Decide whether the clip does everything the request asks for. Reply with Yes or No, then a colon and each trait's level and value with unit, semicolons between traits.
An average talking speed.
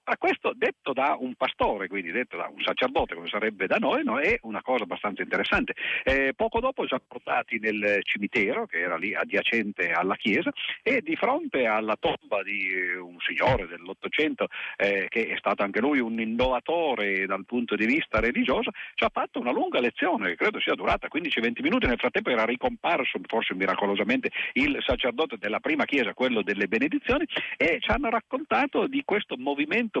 No: fast, 180 wpm